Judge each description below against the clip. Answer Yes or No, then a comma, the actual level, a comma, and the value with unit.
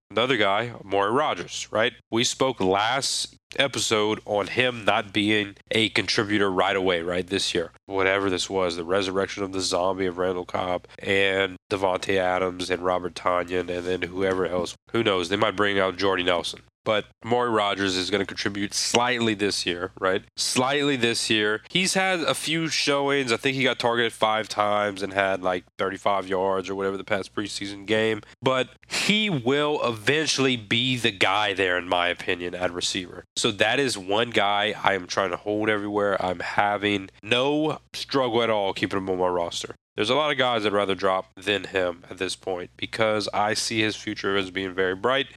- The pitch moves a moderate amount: Yes, average, 3.7 semitones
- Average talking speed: Yes, average, 190 wpm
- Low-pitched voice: Yes, low, 105 Hz